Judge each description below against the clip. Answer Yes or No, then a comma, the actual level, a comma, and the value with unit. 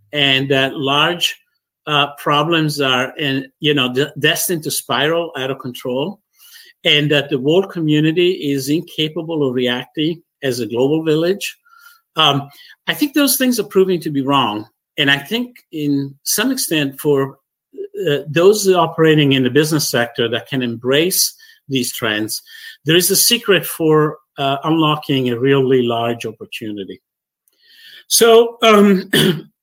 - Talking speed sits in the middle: Yes, average, 145 wpm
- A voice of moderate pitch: Yes, medium, 150 Hz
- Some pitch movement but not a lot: No, wide, 5.7 semitones